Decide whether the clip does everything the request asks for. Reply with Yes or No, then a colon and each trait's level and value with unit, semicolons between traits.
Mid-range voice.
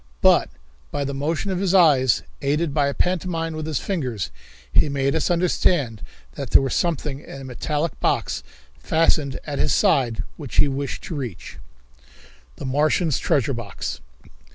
Yes: medium, 145 Hz